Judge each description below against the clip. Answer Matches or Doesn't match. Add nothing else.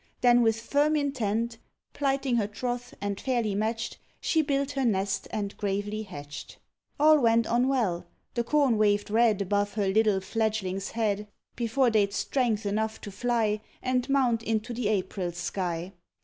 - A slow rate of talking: Doesn't match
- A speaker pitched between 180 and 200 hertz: Doesn't match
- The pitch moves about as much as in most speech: Matches